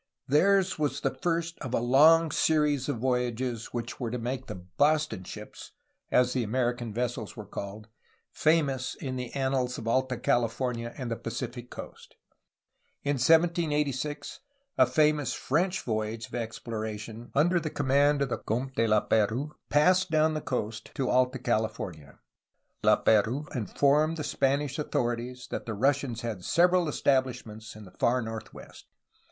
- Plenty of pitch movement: No, average, 4.3 semitones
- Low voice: Yes, low, 130 Hz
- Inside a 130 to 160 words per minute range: Yes, average, 150 wpm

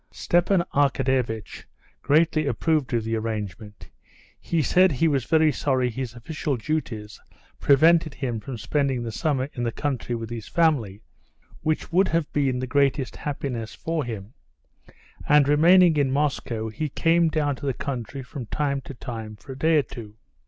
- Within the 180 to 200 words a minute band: No, average, 165 wpm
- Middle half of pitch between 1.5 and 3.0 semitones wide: No, average, 4.7 semitones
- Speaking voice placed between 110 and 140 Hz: Yes, low, 135 Hz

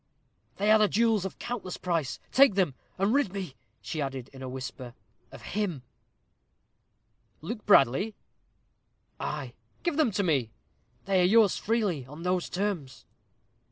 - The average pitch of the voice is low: No, medium, 185 Hz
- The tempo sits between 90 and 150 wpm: Yes, average, 140 wpm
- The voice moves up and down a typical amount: No, wide, 7.1 semitones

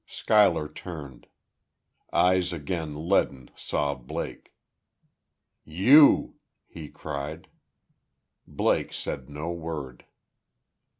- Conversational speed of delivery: No, slow, 75 wpm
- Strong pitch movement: No, average, 3.6 semitones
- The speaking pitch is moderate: No, very low, 80 Hz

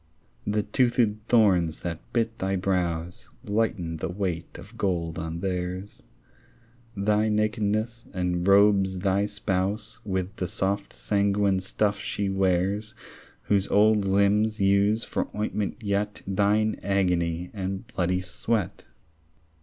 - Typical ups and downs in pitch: No, narrow, 2.3 semitones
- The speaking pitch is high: No, low, 100 Hz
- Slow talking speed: Yes, slow, 115 wpm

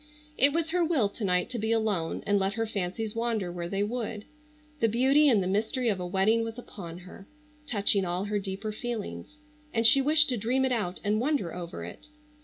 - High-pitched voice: Yes, high, 215 Hz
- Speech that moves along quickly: Yes, fast, 210 wpm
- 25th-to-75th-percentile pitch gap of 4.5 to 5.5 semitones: No, average, 4.0 semitones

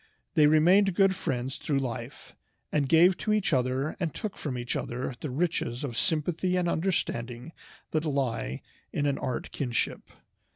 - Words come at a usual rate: Yes, average, 160 wpm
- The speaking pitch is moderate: Yes, medium, 150 Hz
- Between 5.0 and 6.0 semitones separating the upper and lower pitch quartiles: Yes, wide, 5.5 semitones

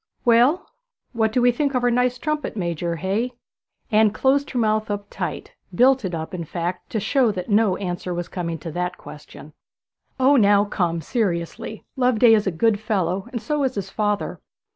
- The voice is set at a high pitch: Yes, high, 215 Hz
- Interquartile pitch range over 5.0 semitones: Yes, wide, 5.4 semitones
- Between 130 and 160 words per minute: No, average, 185 wpm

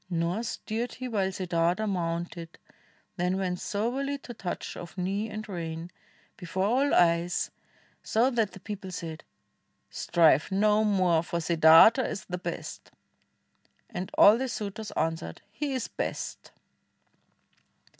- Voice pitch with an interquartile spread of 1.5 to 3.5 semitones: No, average, 4.2 semitones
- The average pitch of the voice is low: No, high, 190 Hz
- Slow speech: Yes, slow, 130 wpm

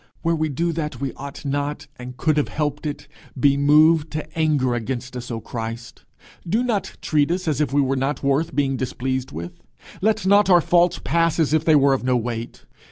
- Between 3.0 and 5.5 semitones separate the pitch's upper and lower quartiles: Yes, average, 3.7 semitones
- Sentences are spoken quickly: Yes, fast, 210 wpm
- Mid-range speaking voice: Yes, medium, 145 Hz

